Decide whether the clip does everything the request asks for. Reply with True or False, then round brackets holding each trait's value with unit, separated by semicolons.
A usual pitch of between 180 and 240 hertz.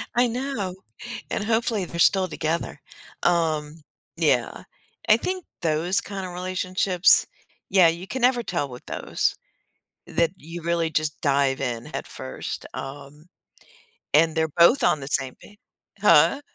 False (170 Hz)